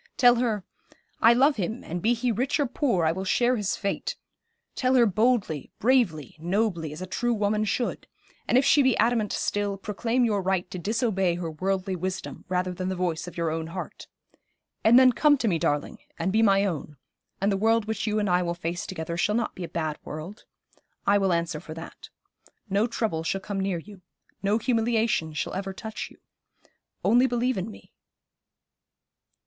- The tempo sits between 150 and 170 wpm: No, average, 195 wpm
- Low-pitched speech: No, high, 200 Hz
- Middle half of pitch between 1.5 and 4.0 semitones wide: No, average, 4.6 semitones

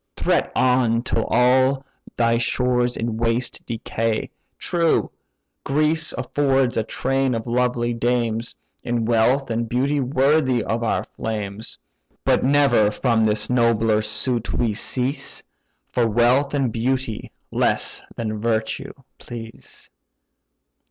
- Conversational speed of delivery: No, slow, 120 wpm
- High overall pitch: No, low, 120 Hz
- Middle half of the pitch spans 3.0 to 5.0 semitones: No, narrow, 2.4 semitones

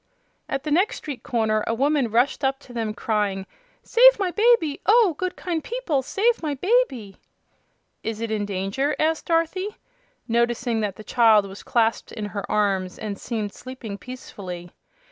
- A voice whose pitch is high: Yes, high, 240 Hz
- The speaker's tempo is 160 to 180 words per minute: Yes, average, 165 wpm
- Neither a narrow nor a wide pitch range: No, wide, 7.3 semitones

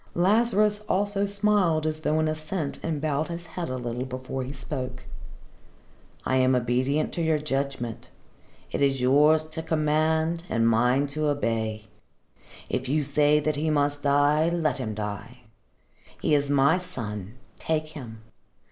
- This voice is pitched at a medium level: Yes, medium, 145 Hz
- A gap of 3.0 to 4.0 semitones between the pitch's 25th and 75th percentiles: Yes, average, 3.6 semitones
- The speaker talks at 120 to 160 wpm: Yes, average, 150 wpm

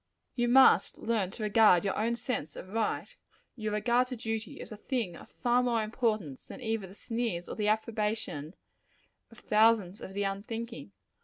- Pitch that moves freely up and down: No, average, 2.7 semitones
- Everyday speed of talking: Yes, average, 175 wpm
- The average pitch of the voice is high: Yes, high, 220 Hz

